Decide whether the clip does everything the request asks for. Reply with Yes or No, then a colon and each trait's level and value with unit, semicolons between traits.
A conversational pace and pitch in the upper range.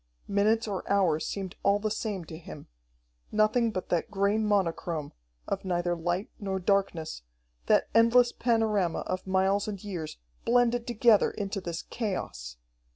Yes: average, 145 wpm; high, 200 Hz